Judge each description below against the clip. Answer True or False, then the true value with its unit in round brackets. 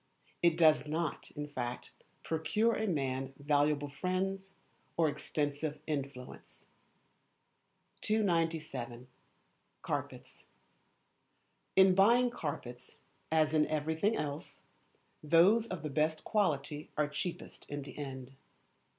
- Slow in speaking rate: True (100 wpm)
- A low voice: False (155 Hz)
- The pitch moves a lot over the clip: False (4.0 semitones)